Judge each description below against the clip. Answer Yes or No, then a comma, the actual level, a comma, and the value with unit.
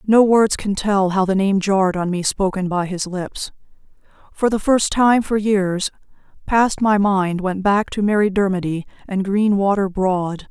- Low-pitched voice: No, high, 195 Hz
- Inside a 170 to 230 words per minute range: Yes, average, 175 wpm